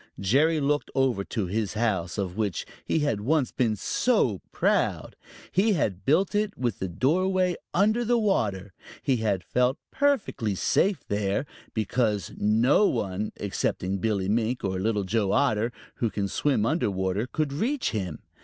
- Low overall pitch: Yes, low, 115 Hz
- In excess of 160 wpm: No, average, 155 wpm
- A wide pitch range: Yes, wide, 6.8 semitones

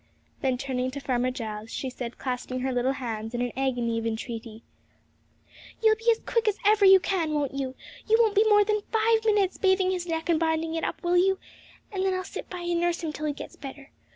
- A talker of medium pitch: No, very high, 320 Hz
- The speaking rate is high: Yes, fast, 225 wpm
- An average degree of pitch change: No, wide, 7.1 semitones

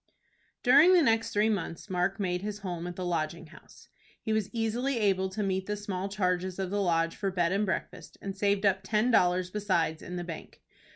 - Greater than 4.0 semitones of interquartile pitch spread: No, average, 2.9 semitones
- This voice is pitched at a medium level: No, high, 195 Hz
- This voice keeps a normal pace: No, fast, 210 wpm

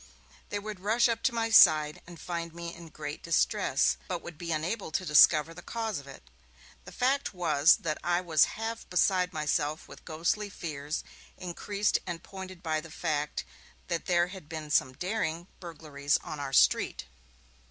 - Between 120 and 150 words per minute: No, average, 175 wpm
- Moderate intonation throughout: Yes, average, 3.5 semitones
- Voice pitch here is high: No, medium, 170 Hz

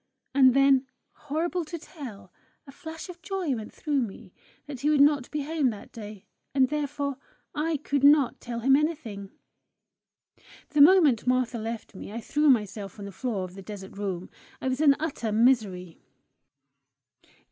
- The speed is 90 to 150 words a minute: No, average, 165 wpm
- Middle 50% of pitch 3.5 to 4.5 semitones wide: No, wide, 5.6 semitones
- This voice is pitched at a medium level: No, very high, 265 Hz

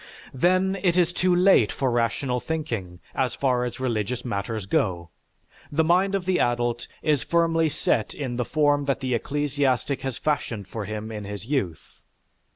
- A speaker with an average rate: Yes, average, 165 wpm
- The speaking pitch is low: Yes, low, 130 Hz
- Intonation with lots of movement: Yes, wide, 5.7 semitones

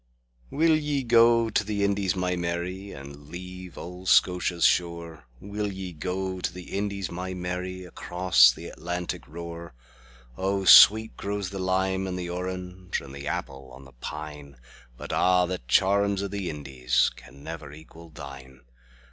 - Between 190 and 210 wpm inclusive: No, slow, 135 wpm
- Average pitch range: Yes, average, 4.4 semitones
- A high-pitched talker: No, very low, 90 Hz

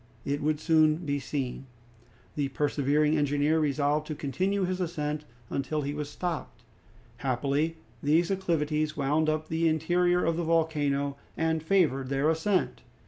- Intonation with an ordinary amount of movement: No, narrow, 2.2 semitones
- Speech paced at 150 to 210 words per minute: No, average, 140 wpm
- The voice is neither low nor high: Yes, medium, 155 Hz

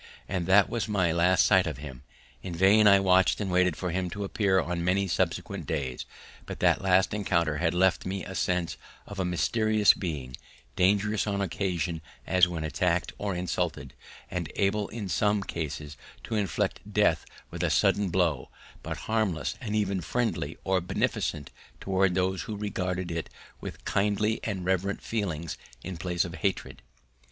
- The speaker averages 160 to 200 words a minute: Yes, average, 170 wpm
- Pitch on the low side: Yes, very low, 95 Hz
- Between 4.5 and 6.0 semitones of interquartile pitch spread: No, average, 2.7 semitones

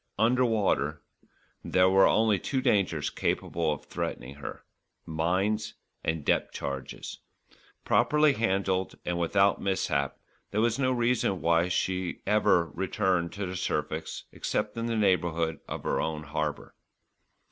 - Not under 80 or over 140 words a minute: Yes, slow, 135 wpm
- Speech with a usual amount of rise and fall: Yes, average, 4.7 semitones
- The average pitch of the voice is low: Yes, very low, 95 Hz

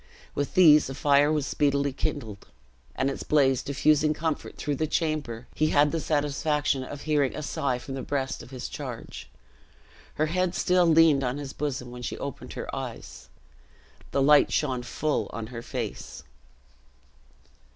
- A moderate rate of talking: Yes, average, 160 wpm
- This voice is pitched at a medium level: Yes, medium, 145 Hz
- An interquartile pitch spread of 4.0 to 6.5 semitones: No, narrow, 2.5 semitones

